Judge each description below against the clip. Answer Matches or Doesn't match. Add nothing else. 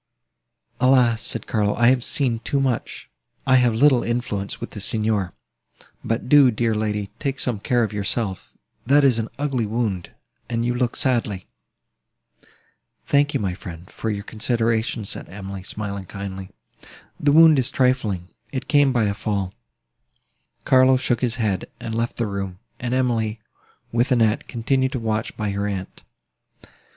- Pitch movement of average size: Matches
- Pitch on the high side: Doesn't match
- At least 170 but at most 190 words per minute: Doesn't match